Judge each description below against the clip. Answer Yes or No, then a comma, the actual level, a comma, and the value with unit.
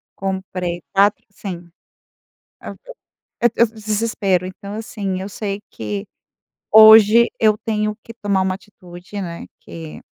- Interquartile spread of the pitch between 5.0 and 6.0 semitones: No, narrow, 2.6 semitones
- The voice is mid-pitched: No, high, 200 Hz